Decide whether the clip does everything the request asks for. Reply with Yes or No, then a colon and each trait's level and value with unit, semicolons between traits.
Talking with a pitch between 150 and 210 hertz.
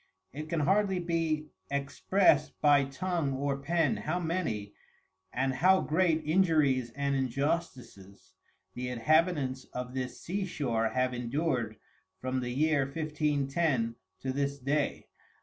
No: medium, 140 Hz